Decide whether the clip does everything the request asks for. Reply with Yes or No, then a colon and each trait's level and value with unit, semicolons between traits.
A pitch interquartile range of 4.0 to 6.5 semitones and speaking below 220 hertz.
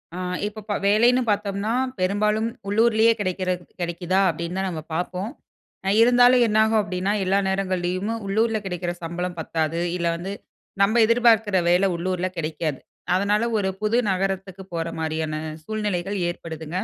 No: average, 3.3 semitones; high, 190 Hz